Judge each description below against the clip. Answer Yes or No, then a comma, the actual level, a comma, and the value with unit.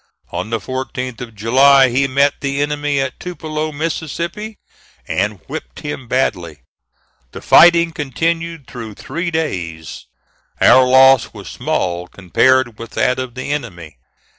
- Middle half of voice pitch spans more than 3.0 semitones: Yes, average, 4.7 semitones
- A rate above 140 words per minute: No, slow, 135 wpm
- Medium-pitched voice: No, low, 130 Hz